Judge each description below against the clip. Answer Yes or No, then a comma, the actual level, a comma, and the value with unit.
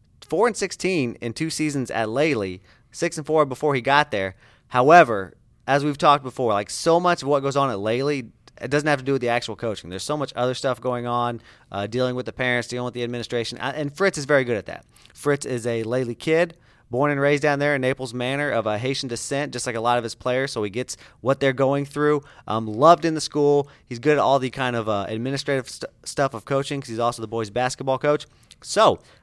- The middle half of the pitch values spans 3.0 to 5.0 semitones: Yes, average, 3.5 semitones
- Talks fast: Yes, fast, 240 wpm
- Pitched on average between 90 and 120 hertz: No, low, 130 Hz